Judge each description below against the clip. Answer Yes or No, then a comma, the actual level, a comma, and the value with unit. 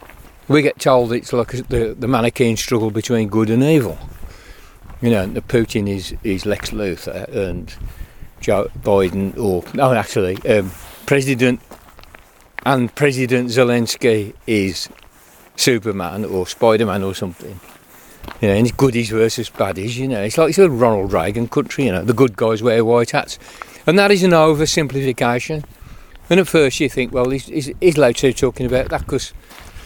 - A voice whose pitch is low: Yes, low, 120 Hz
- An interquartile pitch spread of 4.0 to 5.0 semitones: Yes, average, 4.7 semitones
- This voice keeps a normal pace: Yes, average, 165 wpm